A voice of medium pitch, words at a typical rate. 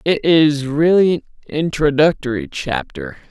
No: medium, 160 Hz; slow, 110 wpm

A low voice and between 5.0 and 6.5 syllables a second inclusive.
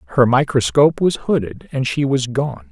Yes: low, 125 Hz; 5.2 syllables/s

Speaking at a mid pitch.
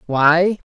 Yes: medium, 165 Hz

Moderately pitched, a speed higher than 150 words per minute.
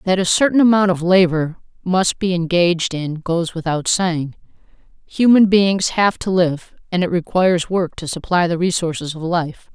Yes: medium, 180 Hz; average, 170 wpm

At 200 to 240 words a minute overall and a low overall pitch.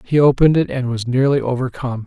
Yes: fast, 205 wpm; low, 130 Hz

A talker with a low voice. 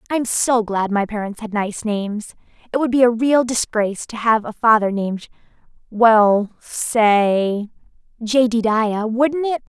No: high, 225 Hz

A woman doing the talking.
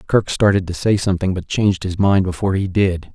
No: male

